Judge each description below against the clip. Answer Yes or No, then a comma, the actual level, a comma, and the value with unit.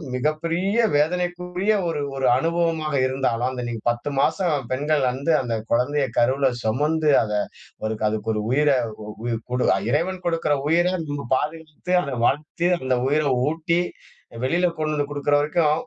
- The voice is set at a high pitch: No, medium, 150 Hz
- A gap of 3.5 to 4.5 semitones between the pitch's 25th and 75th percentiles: Yes, average, 4.1 semitones